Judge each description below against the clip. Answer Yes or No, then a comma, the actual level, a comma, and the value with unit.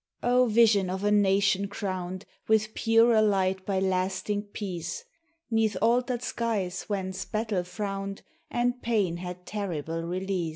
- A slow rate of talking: Yes, slow, 130 wpm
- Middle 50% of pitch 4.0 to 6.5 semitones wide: No, average, 2.8 semitones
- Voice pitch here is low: No, high, 200 Hz